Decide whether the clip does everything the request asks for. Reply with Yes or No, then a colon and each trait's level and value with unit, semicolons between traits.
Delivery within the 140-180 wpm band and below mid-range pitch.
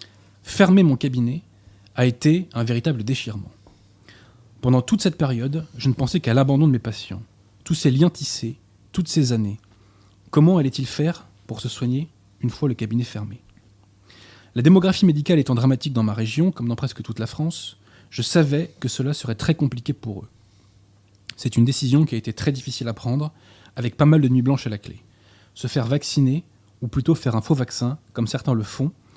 No: average, 190 wpm; low, 120 Hz